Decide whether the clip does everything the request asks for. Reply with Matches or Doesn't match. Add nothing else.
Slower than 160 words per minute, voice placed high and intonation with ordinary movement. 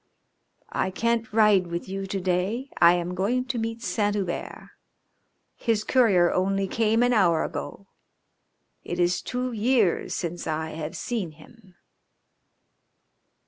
Matches